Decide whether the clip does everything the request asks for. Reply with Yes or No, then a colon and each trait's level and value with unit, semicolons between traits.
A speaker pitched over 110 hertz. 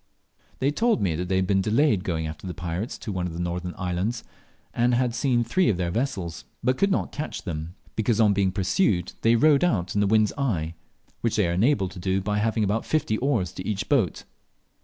No: low, 100 Hz